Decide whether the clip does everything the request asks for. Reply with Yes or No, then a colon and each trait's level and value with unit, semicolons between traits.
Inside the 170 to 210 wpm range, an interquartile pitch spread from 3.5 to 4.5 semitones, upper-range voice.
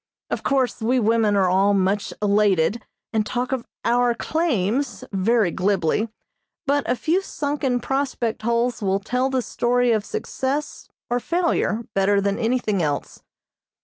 No: average, 145 wpm; average, 4.2 semitones; high, 235 Hz